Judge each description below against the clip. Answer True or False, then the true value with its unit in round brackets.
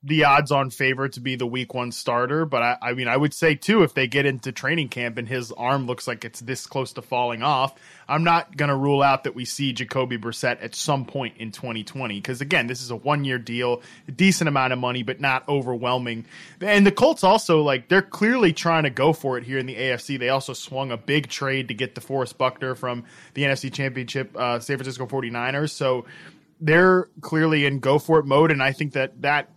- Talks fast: True (225 wpm)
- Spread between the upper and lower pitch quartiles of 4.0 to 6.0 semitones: False (3.1 semitones)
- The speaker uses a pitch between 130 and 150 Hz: True (135 Hz)